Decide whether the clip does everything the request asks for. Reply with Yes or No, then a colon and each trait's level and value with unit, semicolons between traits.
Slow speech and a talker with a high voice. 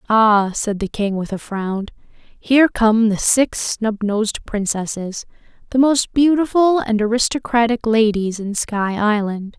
Yes: slow, 130 wpm; high, 220 Hz